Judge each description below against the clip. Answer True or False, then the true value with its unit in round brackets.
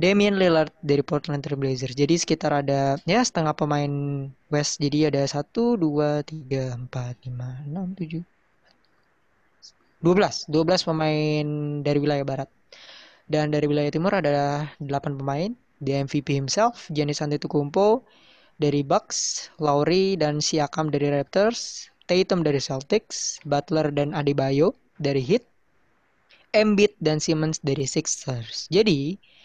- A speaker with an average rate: True (125 wpm)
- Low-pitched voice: False (150 Hz)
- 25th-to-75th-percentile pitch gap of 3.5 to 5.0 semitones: False (2.5 semitones)